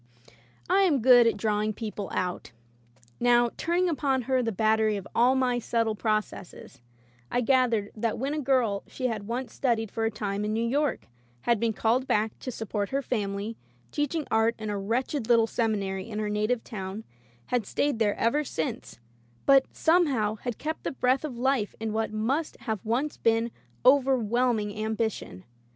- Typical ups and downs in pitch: Yes, average, 3.3 semitones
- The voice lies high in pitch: Yes, high, 230 Hz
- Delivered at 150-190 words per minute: Yes, average, 175 wpm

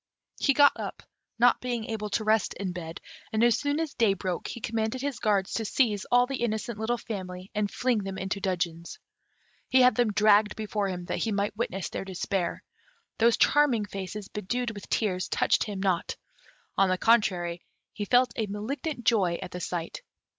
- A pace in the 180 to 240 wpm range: Yes, average, 190 wpm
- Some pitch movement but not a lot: Yes, average, 3.8 semitones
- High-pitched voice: Yes, high, 210 Hz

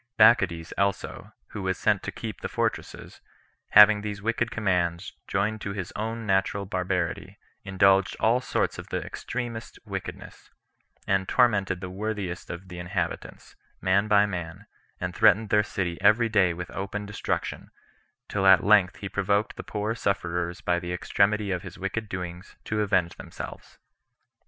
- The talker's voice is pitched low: Yes, low, 100 Hz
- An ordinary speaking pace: Yes, average, 155 wpm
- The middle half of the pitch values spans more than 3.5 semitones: No, average, 2.7 semitones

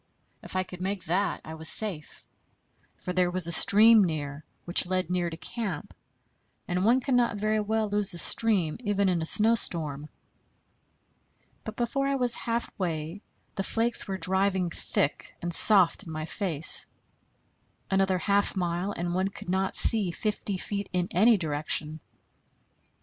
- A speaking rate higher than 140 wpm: Yes, average, 155 wpm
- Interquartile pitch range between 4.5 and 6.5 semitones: No, average, 3.7 semitones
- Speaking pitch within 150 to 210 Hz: Yes, medium, 185 Hz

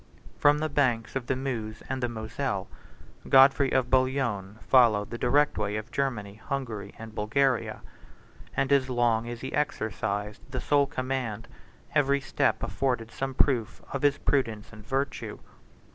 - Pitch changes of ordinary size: Yes, average, 3.7 semitones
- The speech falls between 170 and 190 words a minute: No, average, 150 wpm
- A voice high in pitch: No, low, 125 Hz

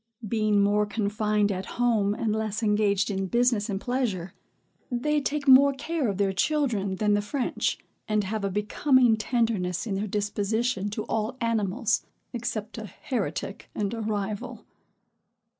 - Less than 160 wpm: Yes, average, 150 wpm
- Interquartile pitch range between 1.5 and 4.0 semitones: Yes, average, 2.9 semitones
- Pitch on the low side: No, high, 215 Hz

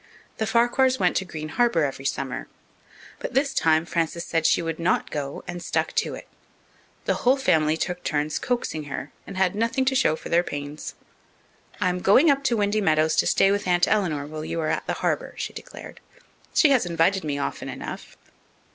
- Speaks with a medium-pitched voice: Yes, medium, 175 Hz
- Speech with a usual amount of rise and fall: No, wide, 6.0 semitones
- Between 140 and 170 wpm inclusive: No, average, 195 wpm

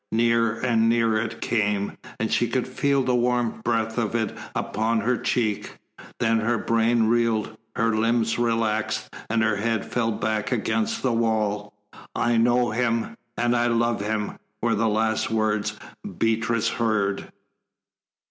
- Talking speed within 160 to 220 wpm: No, average, 150 wpm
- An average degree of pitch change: No, narrow, 1.3 semitones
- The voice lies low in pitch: Yes, low, 115 Hz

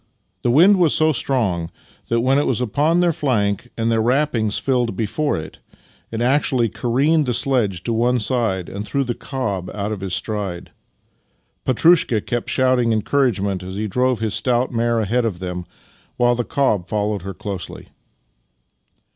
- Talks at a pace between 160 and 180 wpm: Yes, average, 170 wpm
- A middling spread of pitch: Yes, average, 4.2 semitones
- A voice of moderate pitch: No, low, 115 Hz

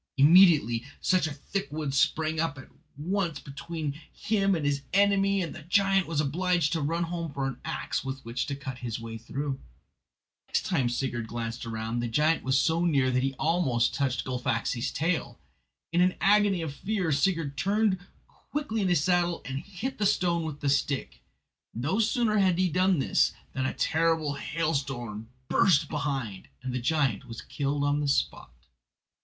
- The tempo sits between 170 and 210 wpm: Yes, average, 180 wpm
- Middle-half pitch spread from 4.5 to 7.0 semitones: Yes, average, 5.2 semitones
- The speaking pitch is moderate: Yes, medium, 150 Hz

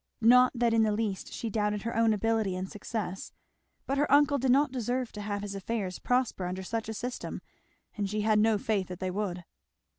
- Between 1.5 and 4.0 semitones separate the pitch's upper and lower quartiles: Yes, average, 2.9 semitones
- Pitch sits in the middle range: No, high, 215 Hz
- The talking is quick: Yes, fast, 210 wpm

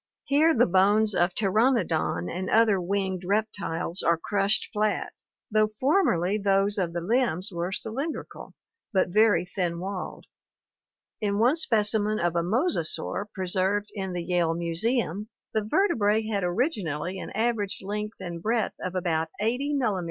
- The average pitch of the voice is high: Yes, high, 200 Hz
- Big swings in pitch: No, average, 3.7 semitones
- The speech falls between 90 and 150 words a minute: Yes, average, 145 wpm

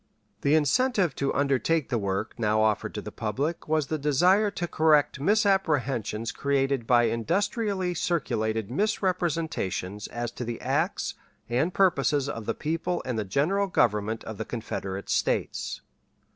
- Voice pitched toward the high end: No, medium, 140 Hz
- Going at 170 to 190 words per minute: No, average, 145 wpm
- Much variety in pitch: Yes, wide, 7.3 semitones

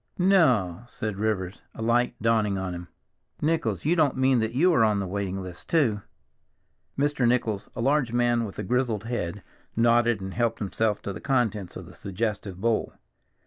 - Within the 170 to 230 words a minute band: Yes, average, 180 wpm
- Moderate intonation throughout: Yes, average, 3.8 semitones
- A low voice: Yes, low, 115 Hz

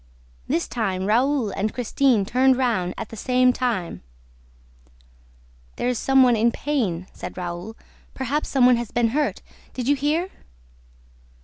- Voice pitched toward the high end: Yes, high, 245 Hz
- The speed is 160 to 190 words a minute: No, average, 145 wpm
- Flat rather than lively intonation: No, average, 3.9 semitones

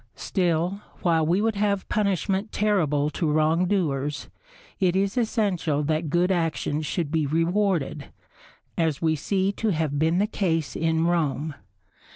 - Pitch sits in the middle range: Yes, medium, 165 Hz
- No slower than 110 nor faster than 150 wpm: Yes, average, 140 wpm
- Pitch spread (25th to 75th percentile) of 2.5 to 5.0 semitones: Yes, average, 3.9 semitones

